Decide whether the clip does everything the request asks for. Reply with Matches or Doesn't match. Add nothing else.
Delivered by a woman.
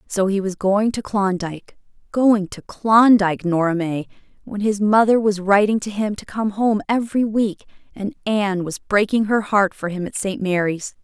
Matches